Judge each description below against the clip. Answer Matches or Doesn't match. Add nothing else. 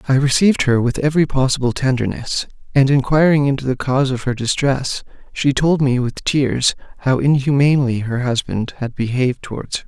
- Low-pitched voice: Matches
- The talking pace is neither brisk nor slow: Matches